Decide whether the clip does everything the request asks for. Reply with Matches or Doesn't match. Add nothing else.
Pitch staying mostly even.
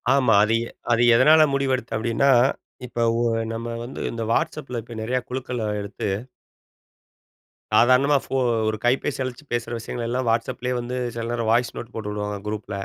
Matches